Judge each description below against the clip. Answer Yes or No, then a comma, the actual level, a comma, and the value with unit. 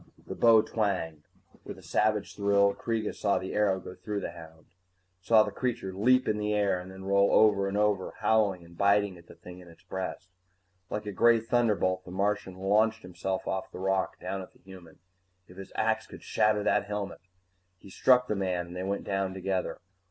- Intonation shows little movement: Yes, narrow, 2.2 semitones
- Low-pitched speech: Yes, low, 100 Hz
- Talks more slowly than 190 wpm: No, fast, 205 wpm